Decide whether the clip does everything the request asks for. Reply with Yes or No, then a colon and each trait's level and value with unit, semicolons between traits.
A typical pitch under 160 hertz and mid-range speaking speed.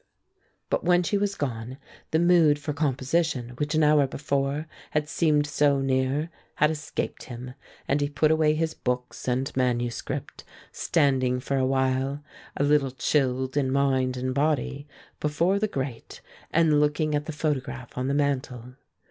Yes: medium, 140 Hz; average, 155 wpm